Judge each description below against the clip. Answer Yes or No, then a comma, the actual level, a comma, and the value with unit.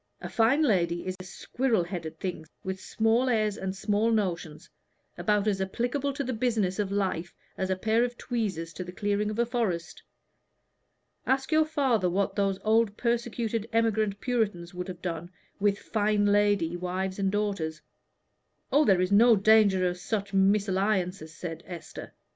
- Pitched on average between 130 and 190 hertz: No, high, 200 Hz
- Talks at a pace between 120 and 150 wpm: No, average, 165 wpm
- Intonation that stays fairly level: No, average, 3.6 semitones